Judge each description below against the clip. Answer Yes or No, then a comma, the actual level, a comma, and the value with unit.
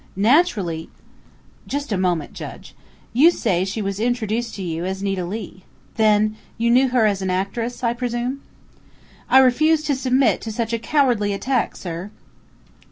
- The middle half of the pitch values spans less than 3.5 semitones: No, average, 4.5 semitones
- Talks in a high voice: Yes, high, 225 Hz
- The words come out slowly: No, average, 165 wpm